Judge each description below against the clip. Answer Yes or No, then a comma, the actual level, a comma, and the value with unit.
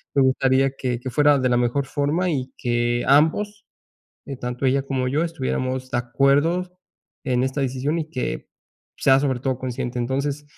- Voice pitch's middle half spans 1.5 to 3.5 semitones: Yes, narrow, 2.4 semitones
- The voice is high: No, low, 135 Hz